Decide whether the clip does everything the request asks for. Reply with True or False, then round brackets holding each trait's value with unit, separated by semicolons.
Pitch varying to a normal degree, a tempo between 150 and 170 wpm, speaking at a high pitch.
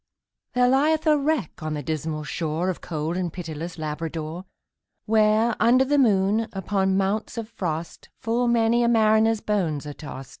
False (6.2 semitones; 160 wpm; 195 Hz)